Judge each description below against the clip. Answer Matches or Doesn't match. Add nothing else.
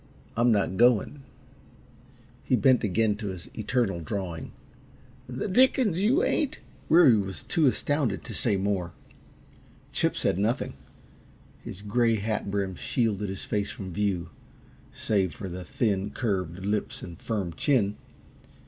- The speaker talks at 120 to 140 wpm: Matches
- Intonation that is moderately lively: Matches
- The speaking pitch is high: Doesn't match